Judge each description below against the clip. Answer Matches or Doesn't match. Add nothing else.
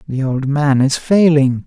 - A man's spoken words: Matches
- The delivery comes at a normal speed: Matches